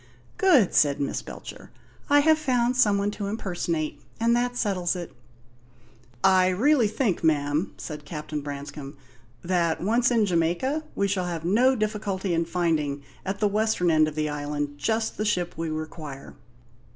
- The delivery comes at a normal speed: Yes, average, 160 wpm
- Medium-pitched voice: Yes, medium, 180 Hz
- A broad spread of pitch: Yes, wide, 5.9 semitones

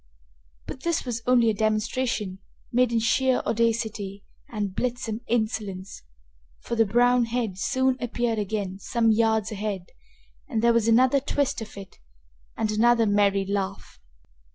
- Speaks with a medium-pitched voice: No, high, 225 Hz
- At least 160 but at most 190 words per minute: No, average, 140 wpm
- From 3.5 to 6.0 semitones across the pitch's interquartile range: No, average, 2.8 semitones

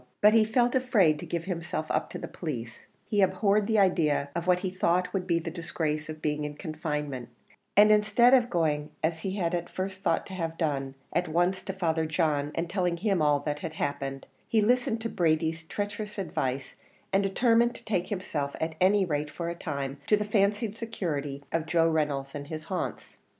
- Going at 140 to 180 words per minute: No, average, 200 wpm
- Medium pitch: Yes, medium, 170 Hz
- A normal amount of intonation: Yes, average, 4.7 semitones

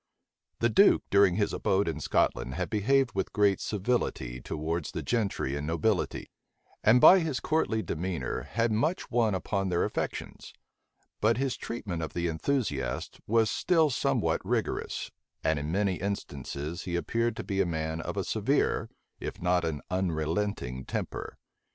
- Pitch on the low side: Yes, very low, 95 Hz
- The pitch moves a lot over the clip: Yes, wide, 6.0 semitones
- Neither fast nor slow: Yes, average, 155 wpm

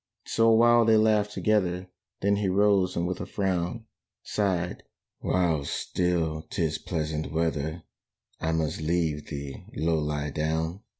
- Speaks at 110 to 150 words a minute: Yes, average, 140 wpm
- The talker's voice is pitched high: No, very low, 85 Hz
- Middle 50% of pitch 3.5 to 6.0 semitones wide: Yes, average, 4.2 semitones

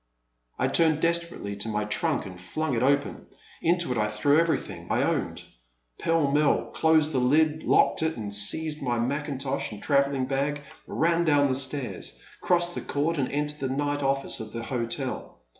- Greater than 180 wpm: No, average, 175 wpm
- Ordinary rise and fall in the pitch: Yes, average, 3.9 semitones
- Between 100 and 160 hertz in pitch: Yes, medium, 140 Hz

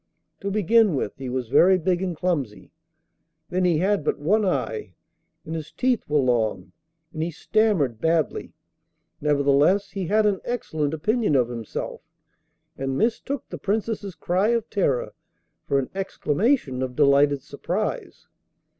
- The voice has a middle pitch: Yes, medium, 165 Hz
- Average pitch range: No, wide, 6.6 semitones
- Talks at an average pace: Yes, average, 145 wpm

